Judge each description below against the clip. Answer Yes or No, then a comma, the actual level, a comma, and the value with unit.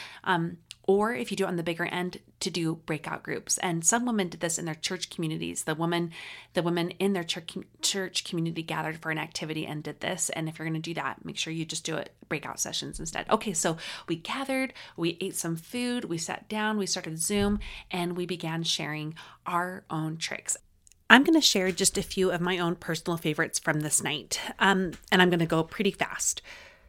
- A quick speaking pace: Yes, fast, 215 wpm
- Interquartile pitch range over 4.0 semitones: No, average, 3.0 semitones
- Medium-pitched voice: Yes, medium, 175 Hz